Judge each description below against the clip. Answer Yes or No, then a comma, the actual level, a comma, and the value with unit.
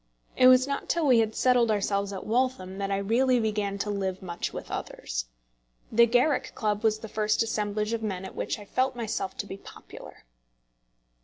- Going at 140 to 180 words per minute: No, average, 190 wpm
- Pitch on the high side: Yes, high, 215 Hz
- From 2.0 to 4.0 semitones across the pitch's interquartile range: Yes, average, 3.3 semitones